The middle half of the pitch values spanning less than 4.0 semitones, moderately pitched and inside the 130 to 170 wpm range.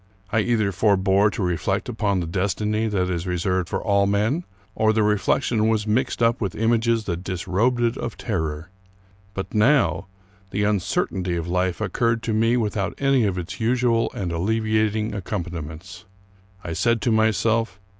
No: average, 3.5 semitones; low, 105 Hz; average, 160 wpm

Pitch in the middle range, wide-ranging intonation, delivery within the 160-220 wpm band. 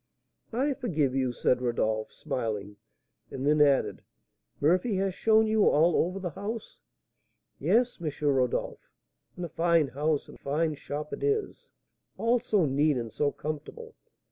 No: medium, 155 Hz; wide, 7.2 semitones; average, 145 wpm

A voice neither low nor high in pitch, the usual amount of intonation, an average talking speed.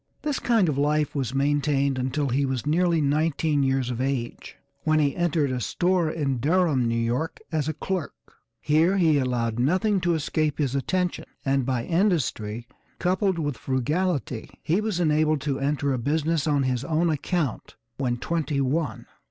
Yes: medium, 145 Hz; average, 3.8 semitones; average, 170 wpm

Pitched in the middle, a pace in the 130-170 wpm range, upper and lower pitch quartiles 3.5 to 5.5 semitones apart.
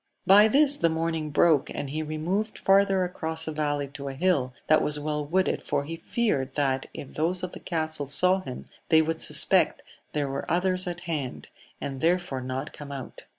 No: medium, 160 Hz; average, 195 wpm; average, 4.0 semitones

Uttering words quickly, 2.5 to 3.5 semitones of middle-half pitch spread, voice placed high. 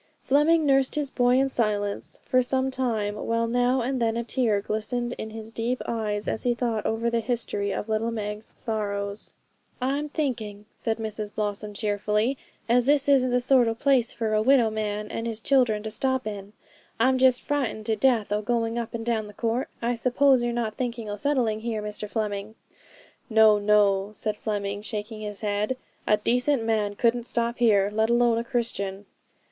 No: average, 185 wpm; average, 2.8 semitones; high, 225 Hz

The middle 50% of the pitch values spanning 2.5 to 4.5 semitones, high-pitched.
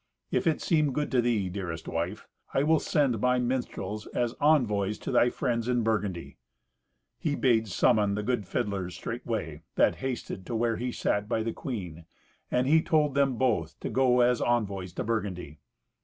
No: average, 4.1 semitones; low, 115 Hz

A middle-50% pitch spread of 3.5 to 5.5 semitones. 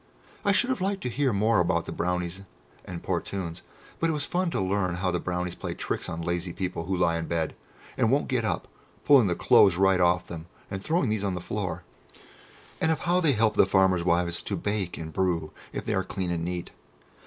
Yes: average, 4.4 semitones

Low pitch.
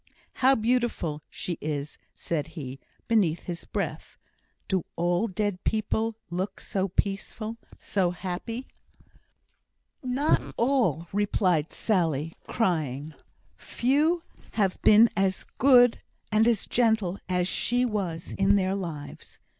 No: high, 195 Hz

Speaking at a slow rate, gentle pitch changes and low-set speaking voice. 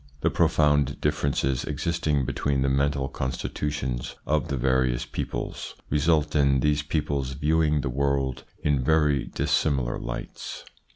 Yes: slow, 125 wpm; narrow, 2.0 semitones; very low, 70 Hz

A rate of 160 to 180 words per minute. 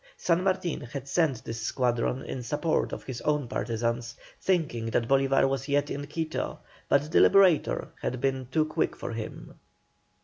Yes: average, 165 wpm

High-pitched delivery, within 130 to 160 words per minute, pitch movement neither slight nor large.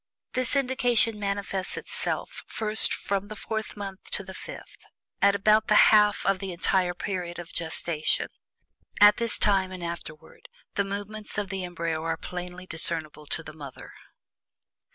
Yes: high, 195 Hz; average, 155 wpm; average, 3.3 semitones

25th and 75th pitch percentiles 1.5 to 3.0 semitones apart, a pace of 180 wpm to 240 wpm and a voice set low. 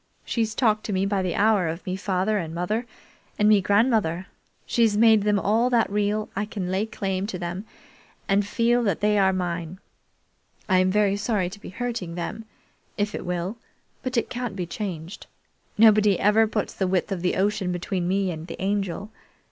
No: narrow, 2.6 semitones; average, 190 wpm; high, 200 Hz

